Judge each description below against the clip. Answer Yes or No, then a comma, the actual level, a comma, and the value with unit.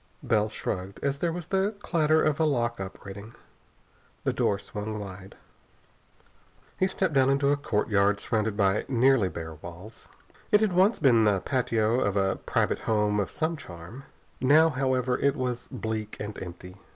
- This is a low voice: Yes, low, 115 Hz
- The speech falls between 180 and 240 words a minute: No, average, 165 wpm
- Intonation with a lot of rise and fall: Yes, wide, 5.7 semitones